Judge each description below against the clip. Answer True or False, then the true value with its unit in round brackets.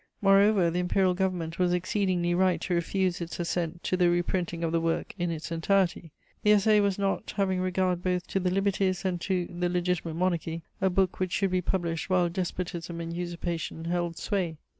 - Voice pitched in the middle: True (180 Hz)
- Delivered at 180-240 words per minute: True (190 wpm)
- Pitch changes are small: True (1.7 semitones)